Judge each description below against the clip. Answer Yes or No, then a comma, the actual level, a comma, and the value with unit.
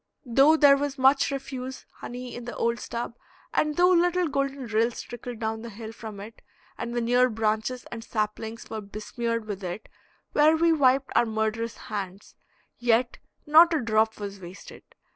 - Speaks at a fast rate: No, average, 170 wpm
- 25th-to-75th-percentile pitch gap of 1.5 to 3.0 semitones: No, average, 3.8 semitones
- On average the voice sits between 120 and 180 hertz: No, high, 235 Hz